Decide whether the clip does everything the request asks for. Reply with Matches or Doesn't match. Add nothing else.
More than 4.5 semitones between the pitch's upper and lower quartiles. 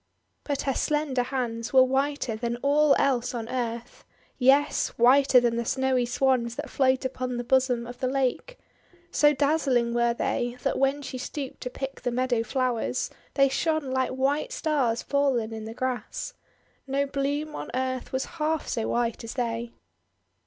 Doesn't match